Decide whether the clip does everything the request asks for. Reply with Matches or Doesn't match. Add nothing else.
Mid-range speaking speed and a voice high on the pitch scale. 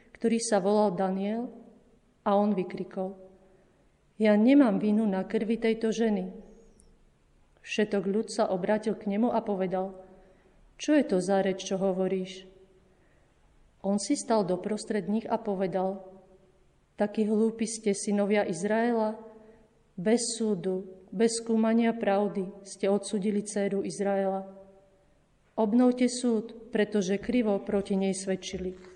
Matches